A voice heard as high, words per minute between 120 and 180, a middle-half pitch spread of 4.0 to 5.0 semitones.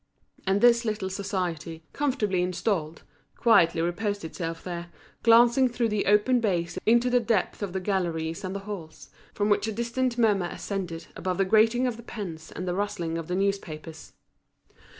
Yes: high, 195 Hz; average, 170 wpm; average, 4.6 semitones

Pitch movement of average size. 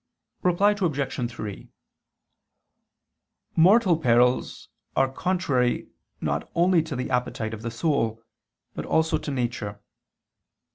No: wide, 6.2 semitones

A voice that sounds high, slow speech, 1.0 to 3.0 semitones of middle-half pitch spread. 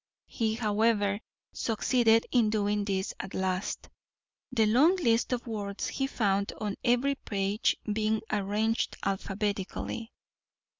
Yes: high, 215 Hz; slow, 115 wpm; narrow, 2.4 semitones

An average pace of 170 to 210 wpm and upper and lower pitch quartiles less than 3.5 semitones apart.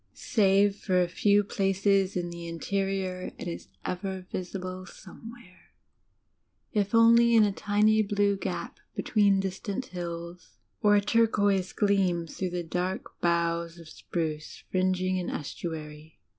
No: slow, 135 wpm; average, 2.7 semitones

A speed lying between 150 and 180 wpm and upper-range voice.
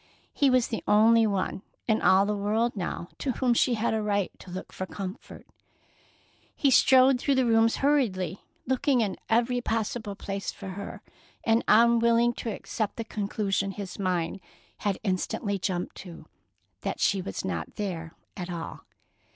Yes: average, 160 wpm; high, 210 Hz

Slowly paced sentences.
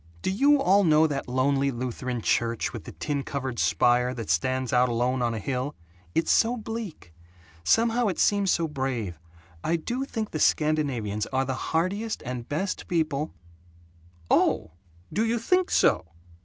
No: average, 165 wpm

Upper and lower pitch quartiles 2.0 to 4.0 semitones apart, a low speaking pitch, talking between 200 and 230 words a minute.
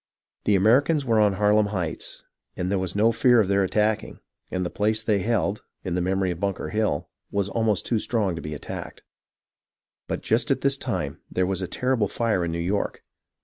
Yes: average, 2.9 semitones; low, 100 Hz; fast, 205 wpm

